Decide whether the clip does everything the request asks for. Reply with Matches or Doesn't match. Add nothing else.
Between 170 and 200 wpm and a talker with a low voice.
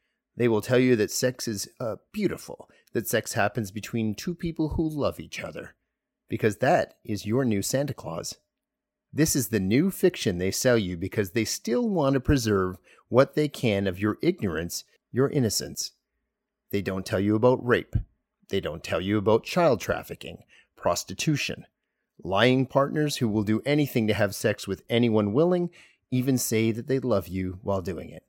Matches